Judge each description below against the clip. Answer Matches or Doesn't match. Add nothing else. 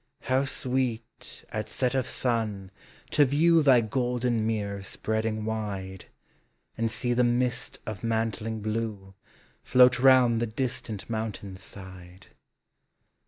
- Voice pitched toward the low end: Matches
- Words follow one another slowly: Matches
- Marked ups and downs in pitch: Doesn't match